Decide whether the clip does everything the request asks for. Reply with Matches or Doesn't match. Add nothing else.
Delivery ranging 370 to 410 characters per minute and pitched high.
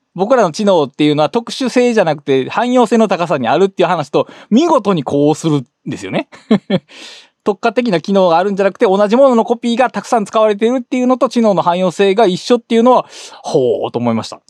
Doesn't match